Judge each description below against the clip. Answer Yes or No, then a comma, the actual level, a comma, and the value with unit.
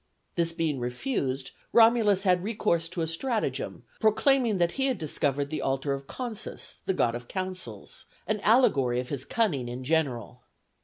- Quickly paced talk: No, average, 160 wpm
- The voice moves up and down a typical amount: No, wide, 8.0 semitones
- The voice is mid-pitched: Yes, medium, 165 Hz